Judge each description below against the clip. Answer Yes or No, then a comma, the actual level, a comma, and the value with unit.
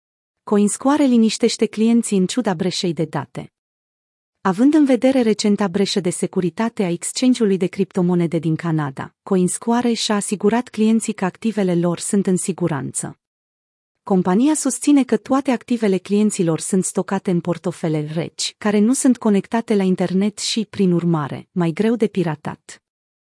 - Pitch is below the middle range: No, high, 200 Hz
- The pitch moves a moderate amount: Yes, average, 4.1 semitones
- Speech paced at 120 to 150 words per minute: Yes, average, 140 wpm